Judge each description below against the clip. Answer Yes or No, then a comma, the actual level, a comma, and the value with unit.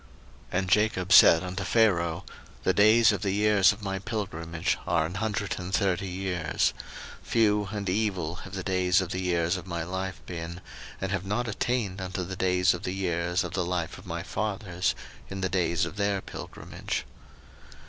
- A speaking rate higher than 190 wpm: No, average, 185 wpm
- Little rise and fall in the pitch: Yes, narrow, 2.3 semitones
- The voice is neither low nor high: No, very low, 95 Hz